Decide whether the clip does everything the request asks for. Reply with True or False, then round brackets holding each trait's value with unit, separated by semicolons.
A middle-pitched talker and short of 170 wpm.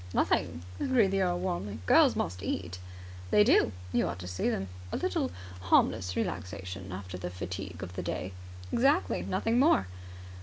False (95 Hz; 160 wpm)